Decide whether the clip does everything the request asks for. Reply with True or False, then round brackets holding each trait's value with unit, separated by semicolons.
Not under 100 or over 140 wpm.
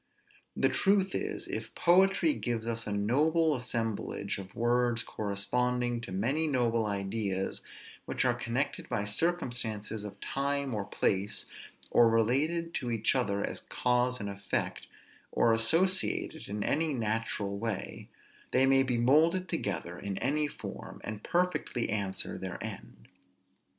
True (135 wpm)